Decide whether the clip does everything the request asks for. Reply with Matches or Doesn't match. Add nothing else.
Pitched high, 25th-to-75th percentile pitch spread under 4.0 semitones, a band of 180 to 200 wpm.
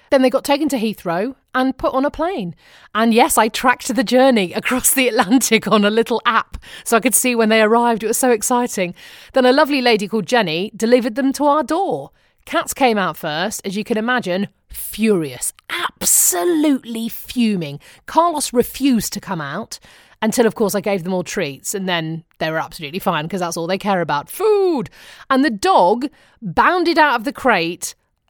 Doesn't match